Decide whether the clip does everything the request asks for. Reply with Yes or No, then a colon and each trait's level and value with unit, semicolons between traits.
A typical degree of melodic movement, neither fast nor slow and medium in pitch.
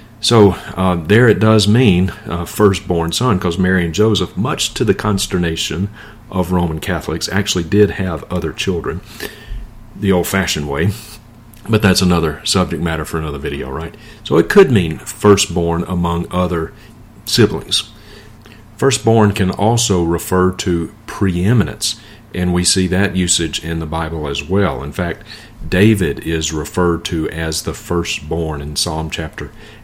No: average, 4.1 semitones; average, 150 wpm; very low, 95 Hz